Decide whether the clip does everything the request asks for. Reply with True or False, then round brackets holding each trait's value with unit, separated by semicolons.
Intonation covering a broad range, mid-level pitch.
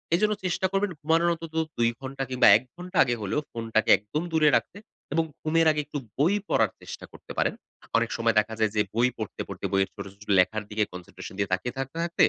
False (7.1 semitones; 130 Hz)